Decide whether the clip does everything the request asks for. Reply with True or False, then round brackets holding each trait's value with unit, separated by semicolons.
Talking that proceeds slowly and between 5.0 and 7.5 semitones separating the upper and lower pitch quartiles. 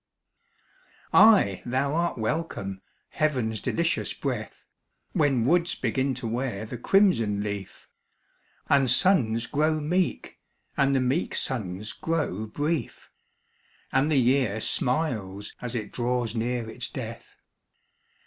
True (115 wpm; 5.6 semitones)